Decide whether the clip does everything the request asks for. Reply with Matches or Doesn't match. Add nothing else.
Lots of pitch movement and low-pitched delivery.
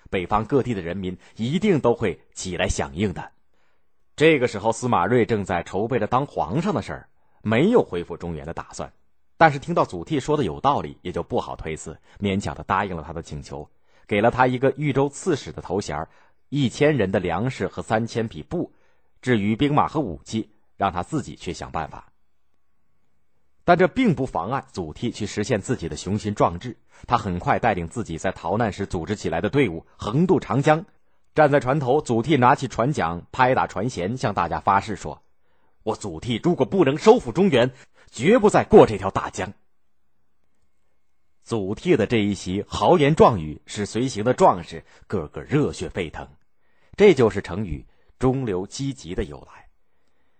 Matches